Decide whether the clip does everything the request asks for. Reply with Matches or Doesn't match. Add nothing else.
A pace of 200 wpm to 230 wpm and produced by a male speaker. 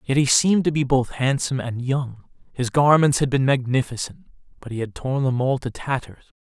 Matches